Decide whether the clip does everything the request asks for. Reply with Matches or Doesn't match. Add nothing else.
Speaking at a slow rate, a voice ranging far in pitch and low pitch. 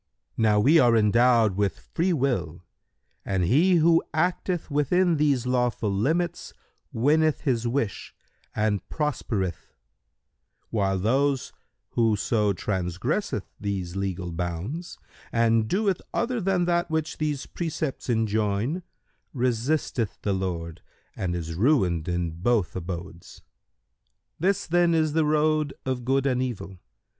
Matches